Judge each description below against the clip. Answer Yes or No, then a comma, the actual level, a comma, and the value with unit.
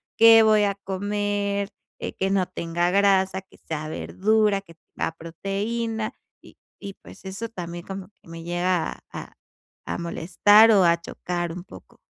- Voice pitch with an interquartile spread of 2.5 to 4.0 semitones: Yes, average, 2.9 semitones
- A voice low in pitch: No, high, 195 Hz